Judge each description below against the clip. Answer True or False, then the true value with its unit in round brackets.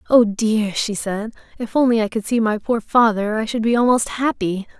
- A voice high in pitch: True (220 Hz)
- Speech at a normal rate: False (215 wpm)